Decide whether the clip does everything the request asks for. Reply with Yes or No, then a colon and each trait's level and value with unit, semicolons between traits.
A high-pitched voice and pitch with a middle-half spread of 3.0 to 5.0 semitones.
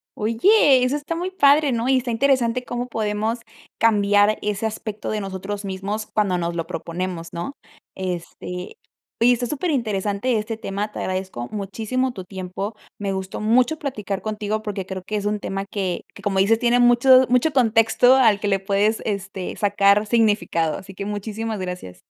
Yes: high, 210 Hz; average, 3.7 semitones